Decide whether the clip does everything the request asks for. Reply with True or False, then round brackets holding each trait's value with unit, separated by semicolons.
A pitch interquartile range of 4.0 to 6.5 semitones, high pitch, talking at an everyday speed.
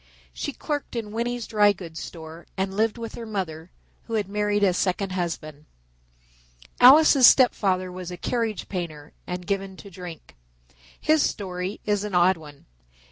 False (3.6 semitones; 195 Hz; 160 wpm)